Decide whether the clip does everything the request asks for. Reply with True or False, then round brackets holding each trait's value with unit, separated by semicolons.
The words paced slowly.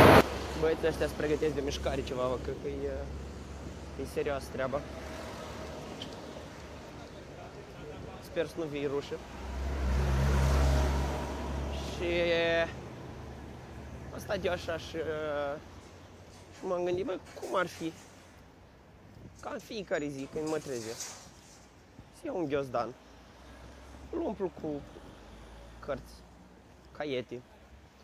True (95 wpm)